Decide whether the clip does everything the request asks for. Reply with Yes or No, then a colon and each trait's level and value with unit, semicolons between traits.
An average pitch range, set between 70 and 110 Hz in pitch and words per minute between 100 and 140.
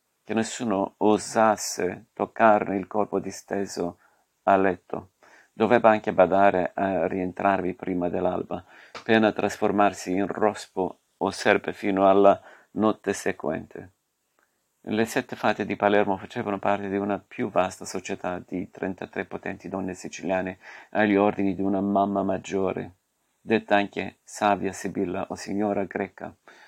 No: narrow, 1.7 semitones; low, 100 Hz; average, 125 wpm